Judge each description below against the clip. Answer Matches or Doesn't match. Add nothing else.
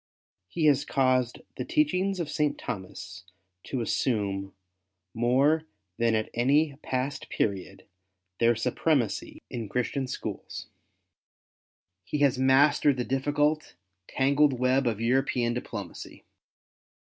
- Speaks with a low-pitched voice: Matches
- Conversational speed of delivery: Doesn't match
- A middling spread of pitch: Matches